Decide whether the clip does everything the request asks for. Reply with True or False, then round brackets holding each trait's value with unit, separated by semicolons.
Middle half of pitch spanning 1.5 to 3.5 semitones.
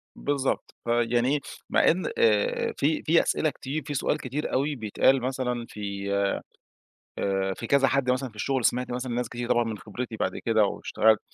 True (2.9 semitones)